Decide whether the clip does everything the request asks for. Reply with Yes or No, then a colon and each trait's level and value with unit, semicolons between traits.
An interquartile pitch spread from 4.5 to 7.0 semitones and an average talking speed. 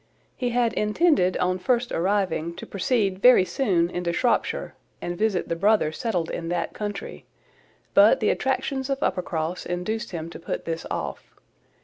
Yes: average, 5.3 semitones; average, 155 wpm